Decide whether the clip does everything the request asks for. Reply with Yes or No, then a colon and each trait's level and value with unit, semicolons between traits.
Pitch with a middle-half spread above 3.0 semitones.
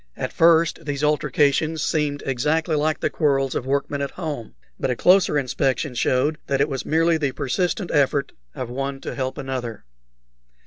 No: average, 2.7 semitones